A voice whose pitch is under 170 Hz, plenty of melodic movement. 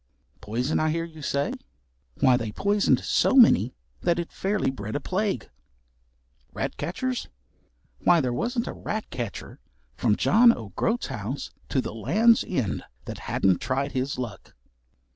Yes: medium, 140 Hz; wide, 8.9 semitones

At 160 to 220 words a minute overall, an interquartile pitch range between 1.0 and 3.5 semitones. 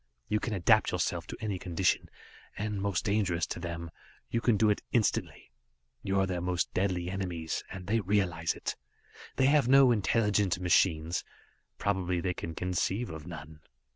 Yes: average, 165 wpm; average, 3.2 semitones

